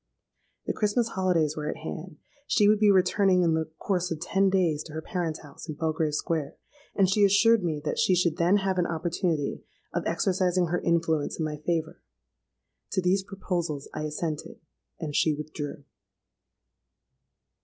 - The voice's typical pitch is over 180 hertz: No, medium, 170 Hz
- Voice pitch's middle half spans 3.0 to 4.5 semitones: Yes, average, 3.4 semitones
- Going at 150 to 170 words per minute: Yes, average, 165 wpm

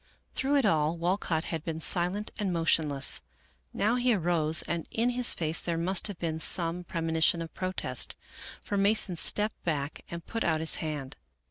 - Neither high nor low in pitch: Yes, medium, 170 Hz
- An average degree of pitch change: Yes, average, 3.9 semitones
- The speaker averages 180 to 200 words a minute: No, average, 170 wpm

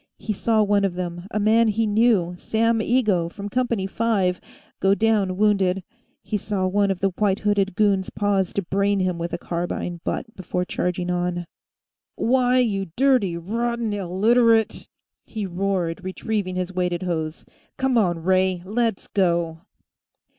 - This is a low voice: No, high, 195 Hz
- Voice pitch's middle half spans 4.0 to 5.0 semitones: No, average, 3.4 semitones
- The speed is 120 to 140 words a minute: No, average, 155 wpm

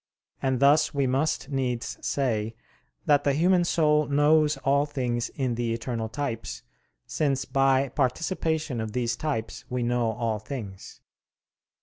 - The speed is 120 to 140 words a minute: Yes, slow, 135 wpm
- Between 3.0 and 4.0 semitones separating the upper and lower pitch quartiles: Yes, average, 3.7 semitones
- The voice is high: No, low, 135 Hz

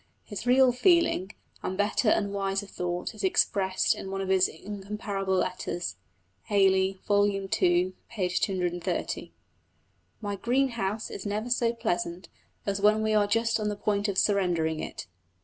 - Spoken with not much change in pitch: Yes, narrow, 2.3 semitones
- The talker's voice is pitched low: No, high, 200 Hz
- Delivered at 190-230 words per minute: No, average, 150 wpm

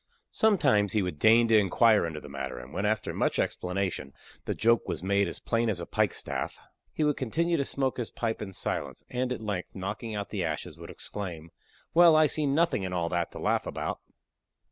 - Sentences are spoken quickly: Yes, fast, 210 wpm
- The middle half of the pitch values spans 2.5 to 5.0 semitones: No, wide, 5.6 semitones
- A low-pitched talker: Yes, low, 105 Hz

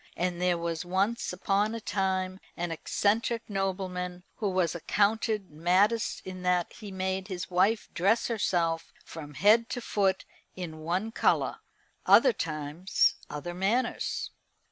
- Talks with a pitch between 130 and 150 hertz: No, medium, 185 Hz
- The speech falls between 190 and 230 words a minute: No, slow, 135 wpm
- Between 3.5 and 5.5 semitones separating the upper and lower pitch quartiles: No, average, 2.9 semitones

